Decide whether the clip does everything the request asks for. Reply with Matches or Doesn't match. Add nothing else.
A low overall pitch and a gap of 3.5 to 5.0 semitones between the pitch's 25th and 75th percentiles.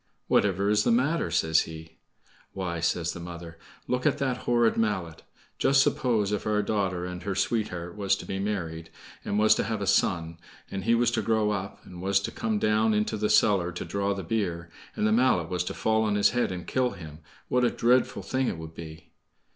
Matches